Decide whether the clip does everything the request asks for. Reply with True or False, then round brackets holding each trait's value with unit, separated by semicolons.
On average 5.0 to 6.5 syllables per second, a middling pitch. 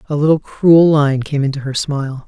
True (5.2 syllables/s; 145 Hz)